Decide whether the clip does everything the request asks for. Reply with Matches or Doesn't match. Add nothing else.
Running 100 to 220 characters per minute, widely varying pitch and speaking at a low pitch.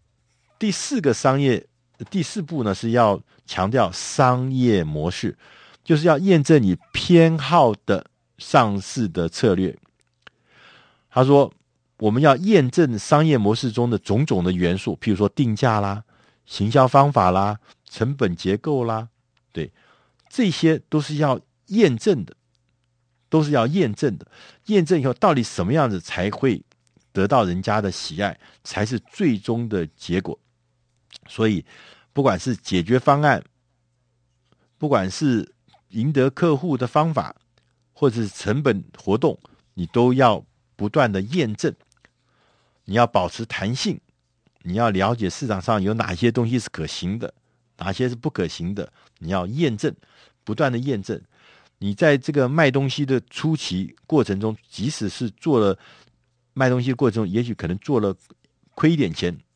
Matches